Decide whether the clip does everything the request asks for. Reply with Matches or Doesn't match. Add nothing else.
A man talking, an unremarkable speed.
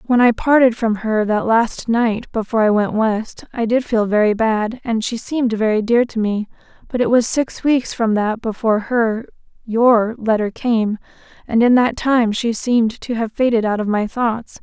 Doesn't match